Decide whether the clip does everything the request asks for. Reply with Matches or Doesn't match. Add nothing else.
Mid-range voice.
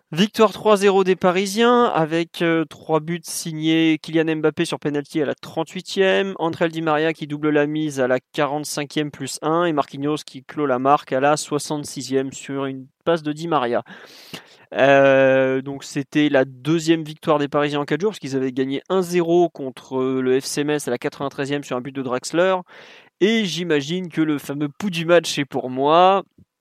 Matches